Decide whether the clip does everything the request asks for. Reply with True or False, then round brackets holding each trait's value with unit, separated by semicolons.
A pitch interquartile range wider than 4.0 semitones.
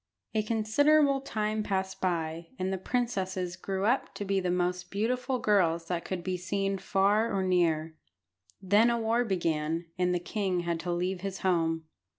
False (3.3 semitones)